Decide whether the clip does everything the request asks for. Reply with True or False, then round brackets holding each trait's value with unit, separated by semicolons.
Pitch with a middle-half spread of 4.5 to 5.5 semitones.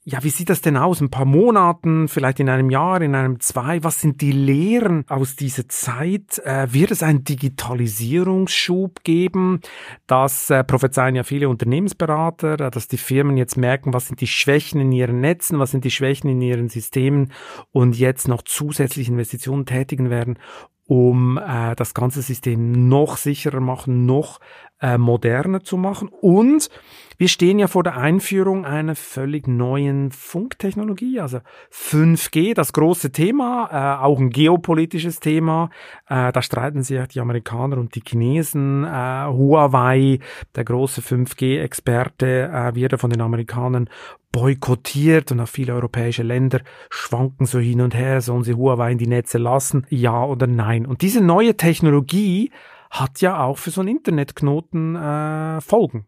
False (4.1 semitones)